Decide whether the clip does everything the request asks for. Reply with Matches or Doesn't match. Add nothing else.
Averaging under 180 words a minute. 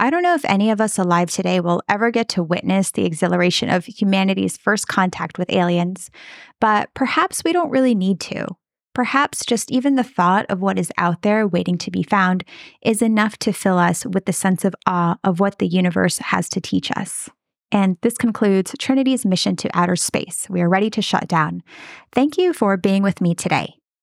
Doesn't match